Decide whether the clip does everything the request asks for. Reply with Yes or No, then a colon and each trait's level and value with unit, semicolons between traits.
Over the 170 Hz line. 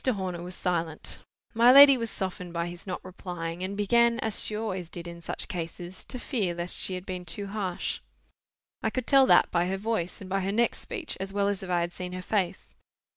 Yes: medium, 185 Hz